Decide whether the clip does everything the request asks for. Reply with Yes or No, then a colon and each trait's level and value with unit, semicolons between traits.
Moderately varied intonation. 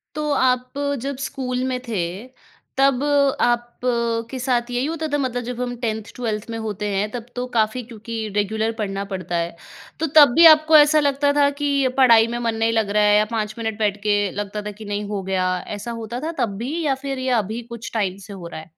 Yes: average, 3.6 semitones